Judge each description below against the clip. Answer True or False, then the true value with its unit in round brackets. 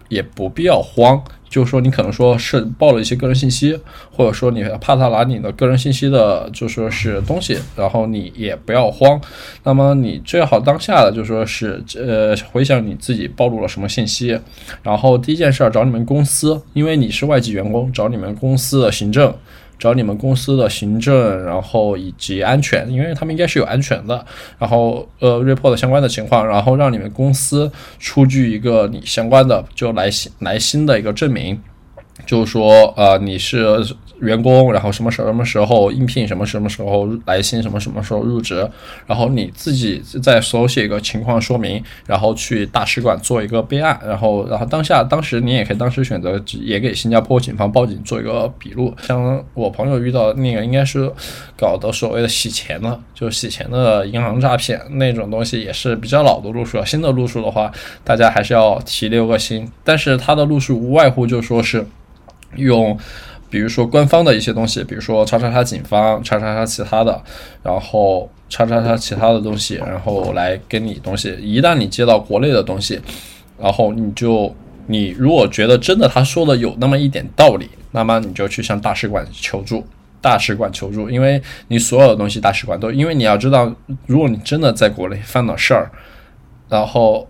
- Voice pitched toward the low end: True (115 Hz)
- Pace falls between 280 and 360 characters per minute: True (310 characters per minute)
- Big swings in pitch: False (3.4 semitones)